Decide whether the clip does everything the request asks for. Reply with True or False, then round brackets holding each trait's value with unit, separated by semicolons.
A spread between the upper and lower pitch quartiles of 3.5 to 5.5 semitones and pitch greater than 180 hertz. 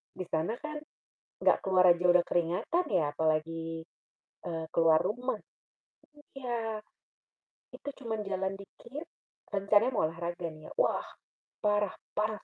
True (5.1 semitones; 190 Hz)